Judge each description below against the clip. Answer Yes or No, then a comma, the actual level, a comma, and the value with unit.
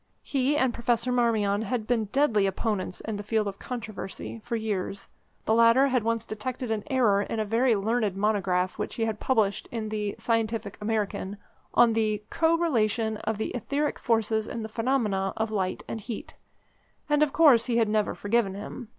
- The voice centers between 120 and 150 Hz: No, high, 220 Hz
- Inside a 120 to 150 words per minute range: No, average, 185 wpm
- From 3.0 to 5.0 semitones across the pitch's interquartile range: No, narrow, 2.5 semitones